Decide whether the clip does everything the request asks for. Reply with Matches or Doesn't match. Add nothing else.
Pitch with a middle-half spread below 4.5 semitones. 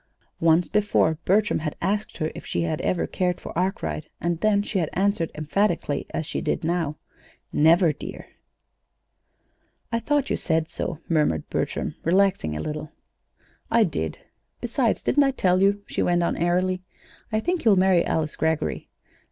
Matches